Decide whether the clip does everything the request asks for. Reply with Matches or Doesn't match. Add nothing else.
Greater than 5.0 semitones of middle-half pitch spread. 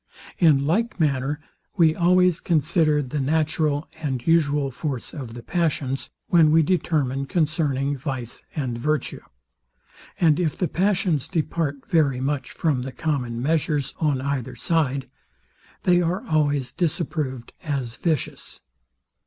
Doesn't match